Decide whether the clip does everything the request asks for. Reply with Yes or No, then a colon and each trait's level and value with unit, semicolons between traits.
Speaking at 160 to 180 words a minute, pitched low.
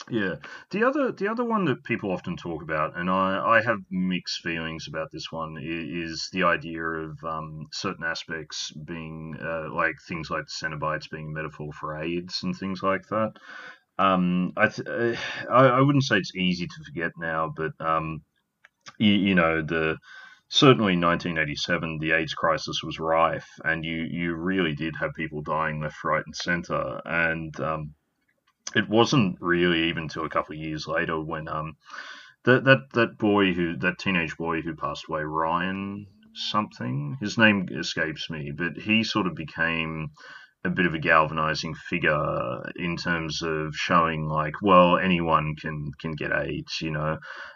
Yes: average, 170 wpm; very low, 80 Hz